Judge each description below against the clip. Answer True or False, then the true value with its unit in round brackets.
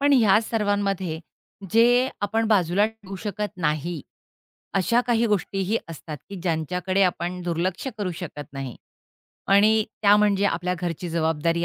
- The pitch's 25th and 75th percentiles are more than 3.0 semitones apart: True (3.7 semitones)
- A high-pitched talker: True (195 Hz)